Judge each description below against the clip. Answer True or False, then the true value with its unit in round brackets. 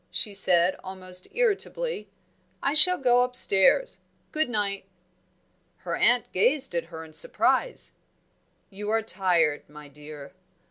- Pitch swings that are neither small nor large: False (7.3 semitones)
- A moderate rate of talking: False (125 wpm)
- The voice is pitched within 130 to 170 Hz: False (200 Hz)